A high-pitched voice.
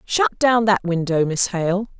Yes: high, 195 Hz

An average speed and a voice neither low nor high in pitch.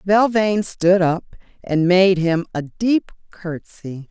No: slow, 130 wpm; medium, 180 Hz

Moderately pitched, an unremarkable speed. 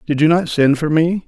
No: medium, 160 Hz; fast, 285 wpm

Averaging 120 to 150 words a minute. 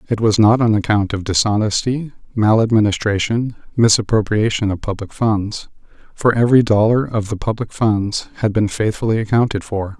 Yes: average, 145 wpm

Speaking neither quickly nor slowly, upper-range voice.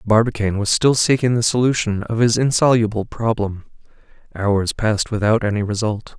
No: average, 145 wpm; low, 110 Hz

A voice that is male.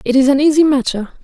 No: female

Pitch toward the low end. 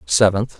Yes: low, 100 Hz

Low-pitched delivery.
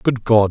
Yes: low, 110 Hz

